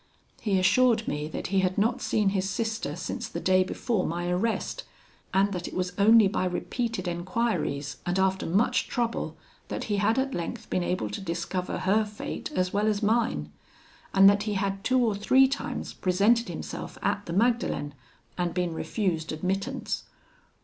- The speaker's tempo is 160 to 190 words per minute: Yes, average, 175 wpm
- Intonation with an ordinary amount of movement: Yes, average, 3.8 semitones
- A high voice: Yes, high, 195 Hz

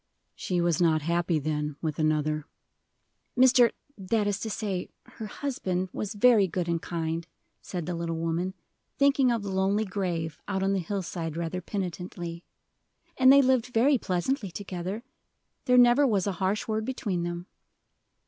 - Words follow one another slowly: No, average, 160 wpm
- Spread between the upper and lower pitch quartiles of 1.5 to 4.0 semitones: No, average, 4.5 semitones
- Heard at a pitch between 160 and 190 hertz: Yes, medium, 185 Hz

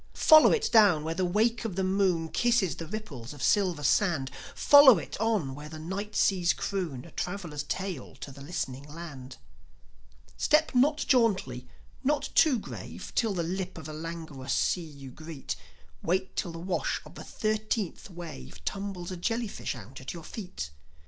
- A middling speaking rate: Yes, average, 170 wpm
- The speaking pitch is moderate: Yes, medium, 175 Hz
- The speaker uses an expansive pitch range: Yes, wide, 5.8 semitones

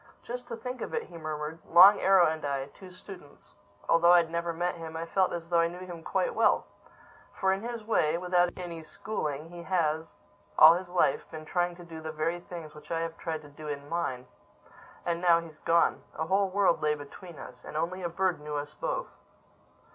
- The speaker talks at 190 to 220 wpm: Yes, average, 195 wpm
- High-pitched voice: No, medium, 170 Hz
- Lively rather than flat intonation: No, narrow, 2.5 semitones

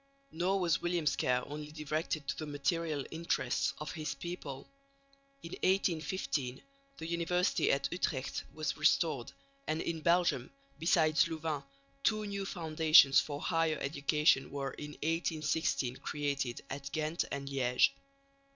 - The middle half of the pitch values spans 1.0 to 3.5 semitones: Yes, average, 3.0 semitones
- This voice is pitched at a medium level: Yes, medium, 155 Hz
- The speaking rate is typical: No, slow, 130 wpm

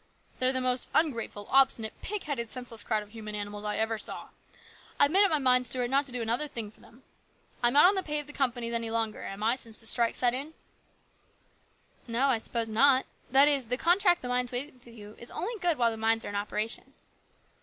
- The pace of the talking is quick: Yes, fast, 235 wpm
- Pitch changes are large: No, average, 3.5 semitones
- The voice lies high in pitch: Yes, high, 245 Hz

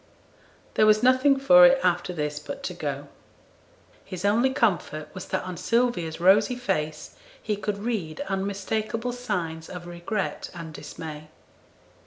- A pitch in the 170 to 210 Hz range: Yes, high, 190 Hz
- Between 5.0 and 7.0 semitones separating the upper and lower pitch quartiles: Yes, wide, 5.6 semitones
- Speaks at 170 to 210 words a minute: No, average, 140 wpm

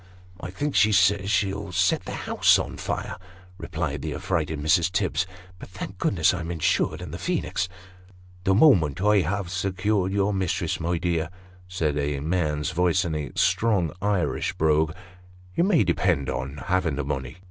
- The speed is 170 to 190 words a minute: Yes, average, 180 wpm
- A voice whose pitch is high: No, very low, 90 Hz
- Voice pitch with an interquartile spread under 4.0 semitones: Yes, average, 3.4 semitones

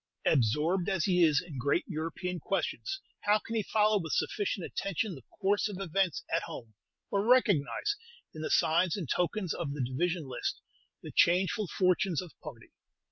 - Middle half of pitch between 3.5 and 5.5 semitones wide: Yes, average, 4.2 semitones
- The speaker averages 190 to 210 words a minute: No, average, 170 wpm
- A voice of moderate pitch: Yes, medium, 180 Hz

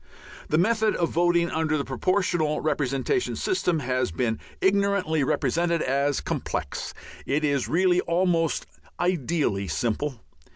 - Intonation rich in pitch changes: No, average, 4.5 semitones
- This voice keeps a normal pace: No, slow, 120 wpm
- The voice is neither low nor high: Yes, medium, 160 Hz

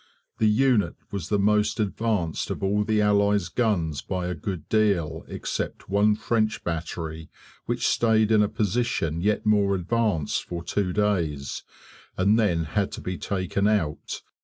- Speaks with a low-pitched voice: Yes, low, 100 Hz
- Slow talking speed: No, average, 155 wpm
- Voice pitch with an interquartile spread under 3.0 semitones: No, average, 3.6 semitones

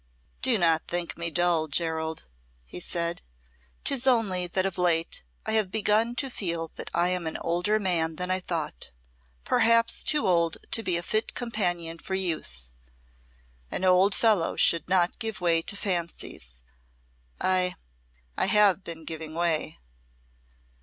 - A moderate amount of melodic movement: Yes, average, 3.4 semitones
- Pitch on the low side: No, medium, 175 Hz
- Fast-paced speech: No, average, 150 wpm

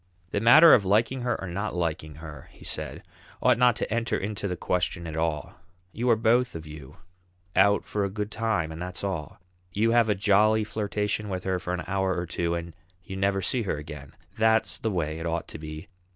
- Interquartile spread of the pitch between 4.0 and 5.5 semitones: Yes, average, 4.5 semitones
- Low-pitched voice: Yes, very low, 95 Hz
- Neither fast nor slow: No, fast, 215 wpm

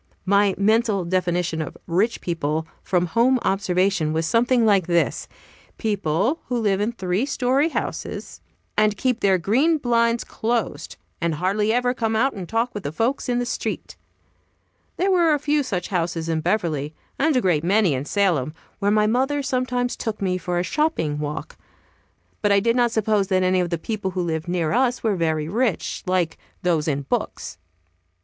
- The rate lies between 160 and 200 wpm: Yes, average, 180 wpm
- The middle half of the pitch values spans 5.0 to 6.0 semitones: Yes, wide, 5.5 semitones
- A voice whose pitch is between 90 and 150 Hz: No, high, 200 Hz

